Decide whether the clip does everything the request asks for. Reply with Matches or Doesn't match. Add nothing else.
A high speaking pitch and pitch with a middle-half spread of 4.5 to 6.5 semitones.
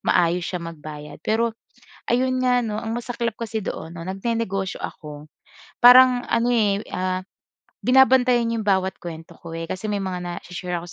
Matches